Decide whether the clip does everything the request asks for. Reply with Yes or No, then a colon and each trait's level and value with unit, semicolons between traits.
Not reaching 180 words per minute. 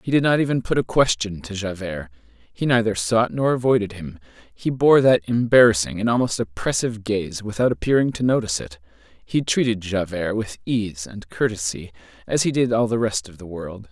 No: average, 190 wpm